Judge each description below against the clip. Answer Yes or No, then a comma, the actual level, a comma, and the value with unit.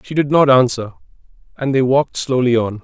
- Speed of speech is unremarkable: Yes, average, 190 wpm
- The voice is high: No, low, 130 Hz